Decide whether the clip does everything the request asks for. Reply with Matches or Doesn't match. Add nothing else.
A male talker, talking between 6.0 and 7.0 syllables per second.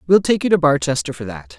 Matches